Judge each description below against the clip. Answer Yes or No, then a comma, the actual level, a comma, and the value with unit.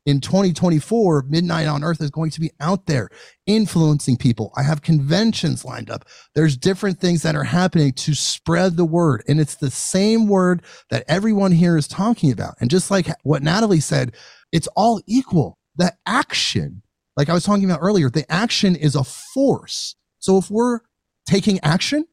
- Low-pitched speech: No, medium, 165 Hz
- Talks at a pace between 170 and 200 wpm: Yes, average, 180 wpm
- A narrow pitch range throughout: No, average, 4.7 semitones